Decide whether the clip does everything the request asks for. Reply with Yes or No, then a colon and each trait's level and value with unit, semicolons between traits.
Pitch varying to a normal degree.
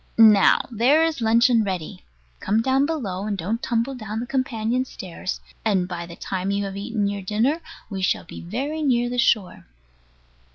Yes: average, 4.1 semitones